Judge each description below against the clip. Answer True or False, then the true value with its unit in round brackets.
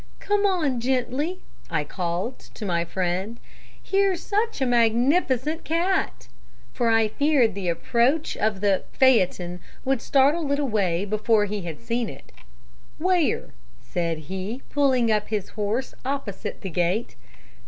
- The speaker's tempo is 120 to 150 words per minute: True (135 wpm)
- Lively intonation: True (6.7 semitones)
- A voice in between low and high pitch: False (230 Hz)